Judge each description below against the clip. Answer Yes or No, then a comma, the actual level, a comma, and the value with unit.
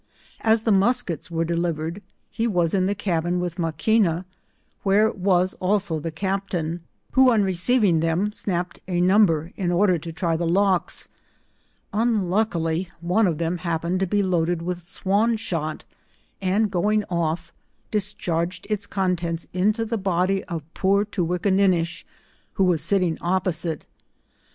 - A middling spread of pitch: Yes, average, 3.1 semitones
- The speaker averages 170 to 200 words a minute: No, average, 140 wpm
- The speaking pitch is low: No, medium, 180 Hz